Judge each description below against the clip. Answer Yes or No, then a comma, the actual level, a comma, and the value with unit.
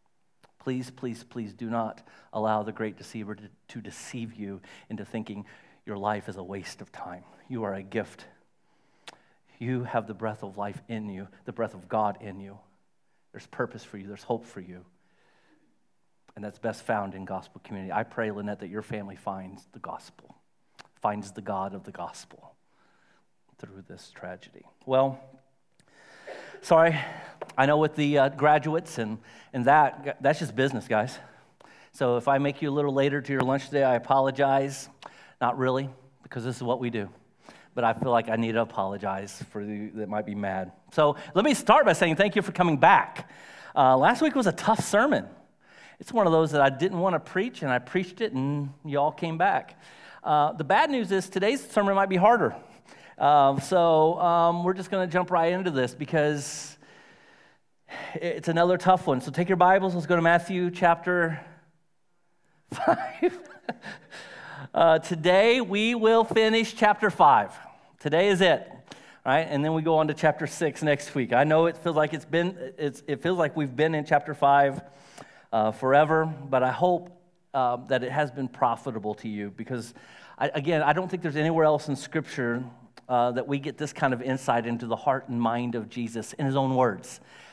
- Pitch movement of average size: No, wide, 6.3 semitones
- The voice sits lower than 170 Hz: Yes, medium, 140 Hz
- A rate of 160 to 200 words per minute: Yes, average, 190 wpm